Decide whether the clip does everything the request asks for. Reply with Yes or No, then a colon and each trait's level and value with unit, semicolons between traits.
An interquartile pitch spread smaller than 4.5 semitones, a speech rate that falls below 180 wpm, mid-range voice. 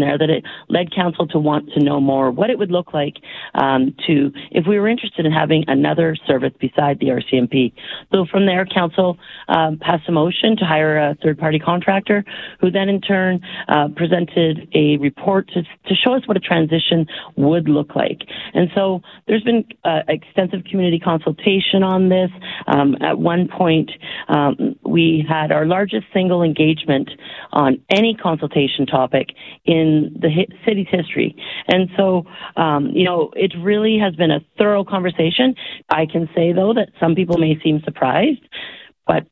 Yes: average, 3.8 semitones; average, 170 wpm; medium, 170 Hz